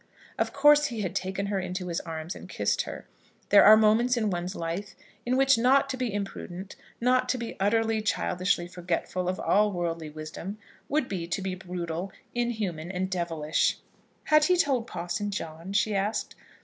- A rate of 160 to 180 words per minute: Yes, average, 175 wpm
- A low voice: No, high, 195 Hz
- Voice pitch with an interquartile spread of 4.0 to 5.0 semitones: Yes, average, 4.6 semitones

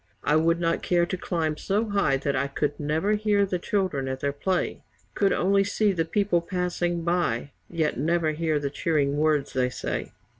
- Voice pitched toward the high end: No, medium, 165 Hz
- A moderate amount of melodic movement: Yes, average, 4.2 semitones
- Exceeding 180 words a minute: Yes, average, 190 wpm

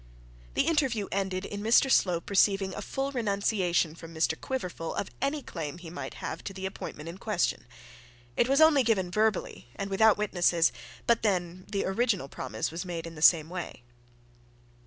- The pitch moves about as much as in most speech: Yes, average, 4.3 semitones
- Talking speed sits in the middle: Yes, average, 175 wpm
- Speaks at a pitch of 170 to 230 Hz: Yes, high, 190 Hz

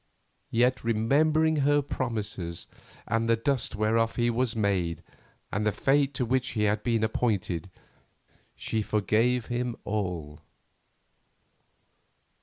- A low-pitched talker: Yes, low, 115 Hz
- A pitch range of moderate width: Yes, average, 3.0 semitones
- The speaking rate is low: Yes, slow, 115 wpm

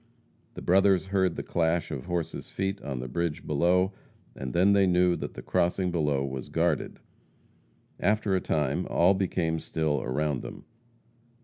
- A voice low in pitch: Yes, very low, 85 Hz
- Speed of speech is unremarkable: Yes, average, 155 wpm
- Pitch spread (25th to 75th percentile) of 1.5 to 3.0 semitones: No, average, 3.9 semitones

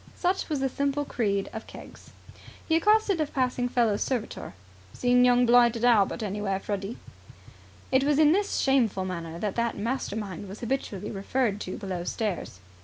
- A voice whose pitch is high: Yes, high, 235 Hz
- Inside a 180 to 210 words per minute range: No, average, 160 wpm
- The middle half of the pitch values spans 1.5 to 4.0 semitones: No, average, 5.0 semitones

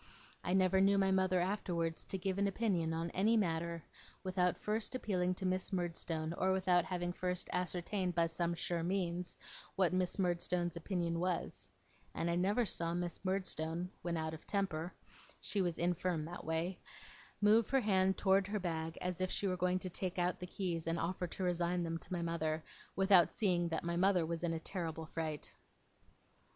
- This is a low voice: No, medium, 180 Hz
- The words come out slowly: No, average, 185 wpm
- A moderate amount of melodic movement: No, narrow, 2.1 semitones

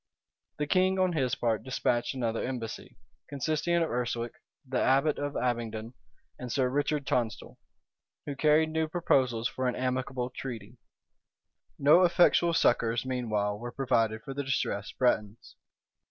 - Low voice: Yes, low, 130 Hz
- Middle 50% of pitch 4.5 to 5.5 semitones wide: No, average, 3.7 semitones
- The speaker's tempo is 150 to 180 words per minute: No, average, 140 wpm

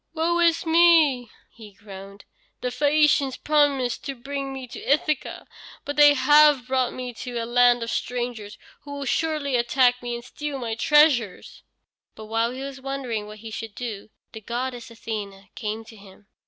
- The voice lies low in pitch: No, very high, 250 Hz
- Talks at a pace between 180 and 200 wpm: No, average, 170 wpm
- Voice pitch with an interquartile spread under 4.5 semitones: Yes, average, 4.0 semitones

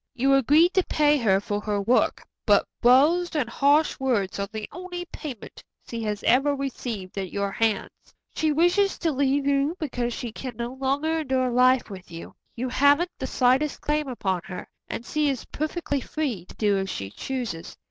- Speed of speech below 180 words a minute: No, average, 185 wpm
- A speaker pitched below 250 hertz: No, very high, 260 Hz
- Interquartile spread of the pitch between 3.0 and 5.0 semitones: No, wide, 5.4 semitones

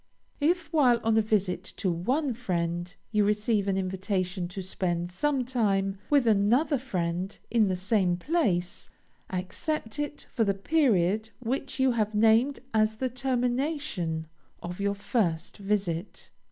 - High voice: Yes, high, 210 Hz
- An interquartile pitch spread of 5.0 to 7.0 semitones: Yes, wide, 5.4 semitones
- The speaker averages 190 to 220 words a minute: No, average, 140 wpm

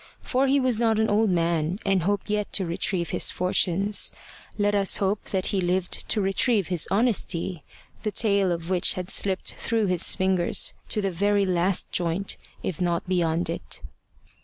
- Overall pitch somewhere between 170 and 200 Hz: Yes, high, 190 Hz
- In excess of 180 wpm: No, average, 175 wpm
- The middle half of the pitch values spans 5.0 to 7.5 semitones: No, average, 2.7 semitones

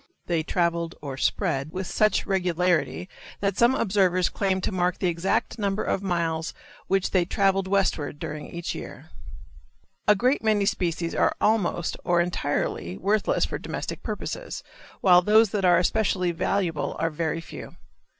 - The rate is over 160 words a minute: No, average, 150 wpm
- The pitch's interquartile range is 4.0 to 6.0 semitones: No, average, 2.8 semitones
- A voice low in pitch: No, medium, 180 Hz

